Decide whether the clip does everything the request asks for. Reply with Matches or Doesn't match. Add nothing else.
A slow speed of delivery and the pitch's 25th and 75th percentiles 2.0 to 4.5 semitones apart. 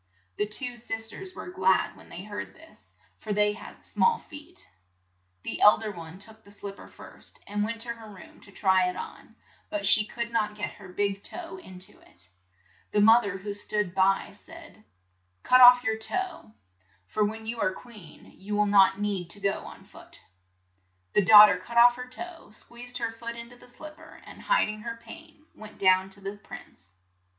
Doesn't match